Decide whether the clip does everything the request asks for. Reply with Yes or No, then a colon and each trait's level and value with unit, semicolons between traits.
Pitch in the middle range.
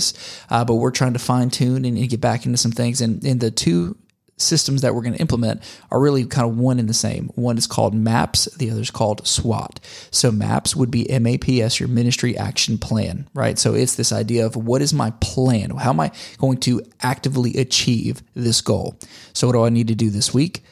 No: low, 120 Hz